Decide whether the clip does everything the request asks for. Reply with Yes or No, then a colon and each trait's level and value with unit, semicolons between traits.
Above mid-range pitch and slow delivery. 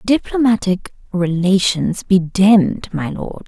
Yes: high, 195 Hz; slow, 105 wpm